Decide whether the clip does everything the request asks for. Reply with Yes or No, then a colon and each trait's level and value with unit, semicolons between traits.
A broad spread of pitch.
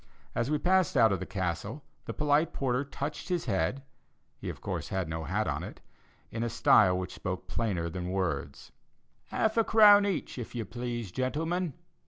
Yes: wide, 8.5 semitones